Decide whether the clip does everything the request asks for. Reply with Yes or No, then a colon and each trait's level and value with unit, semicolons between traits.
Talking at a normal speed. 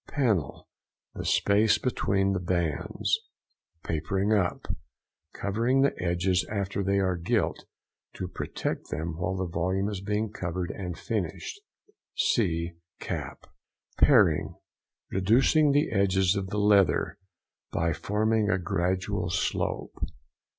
No: slow, 110 wpm